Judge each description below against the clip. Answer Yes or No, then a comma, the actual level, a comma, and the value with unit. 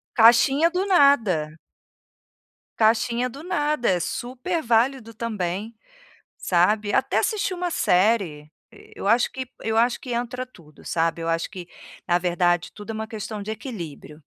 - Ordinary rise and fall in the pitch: No, wide, 6.1 semitones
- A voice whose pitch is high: Yes, high, 225 Hz